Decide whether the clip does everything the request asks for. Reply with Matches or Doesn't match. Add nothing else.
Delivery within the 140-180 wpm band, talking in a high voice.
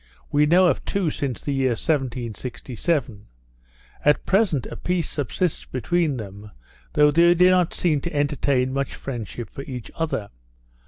Doesn't match